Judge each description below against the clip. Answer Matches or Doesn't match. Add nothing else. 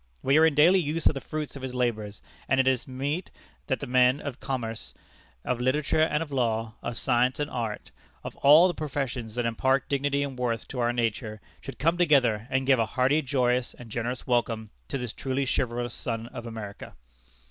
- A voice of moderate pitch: Doesn't match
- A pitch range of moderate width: Matches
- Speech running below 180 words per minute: Doesn't match